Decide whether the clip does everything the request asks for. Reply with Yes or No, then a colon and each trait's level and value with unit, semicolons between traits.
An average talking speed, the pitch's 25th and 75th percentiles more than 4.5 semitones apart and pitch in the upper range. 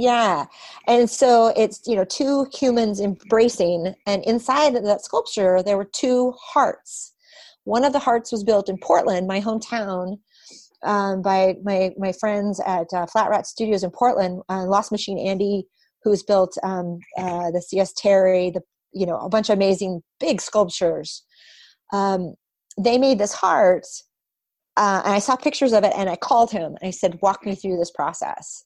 No: average, 175 wpm; average, 3.5 semitones; high, 200 Hz